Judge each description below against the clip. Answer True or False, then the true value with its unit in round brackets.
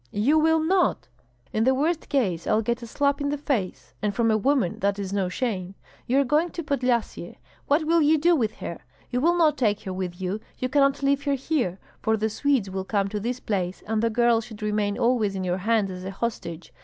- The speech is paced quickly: True (230 wpm)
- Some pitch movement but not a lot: False (6.0 semitones)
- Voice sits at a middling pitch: False (230 Hz)